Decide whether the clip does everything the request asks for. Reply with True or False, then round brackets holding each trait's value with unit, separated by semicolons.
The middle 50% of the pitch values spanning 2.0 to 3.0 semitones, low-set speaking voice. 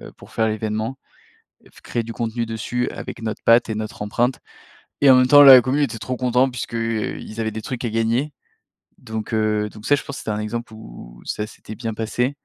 True (2.4 semitones; 115 Hz)